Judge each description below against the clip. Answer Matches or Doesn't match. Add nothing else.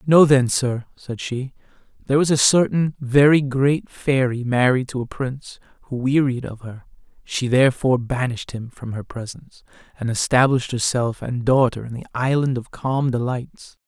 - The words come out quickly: Doesn't match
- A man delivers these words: Matches